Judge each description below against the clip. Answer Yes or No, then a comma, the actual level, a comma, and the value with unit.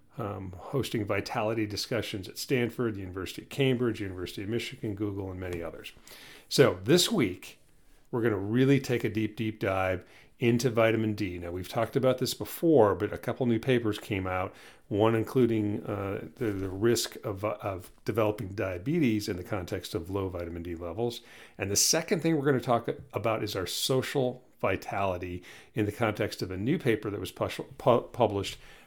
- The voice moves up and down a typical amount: Yes, average, 3.5 semitones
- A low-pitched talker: Yes, low, 110 Hz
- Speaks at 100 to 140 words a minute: No, average, 185 wpm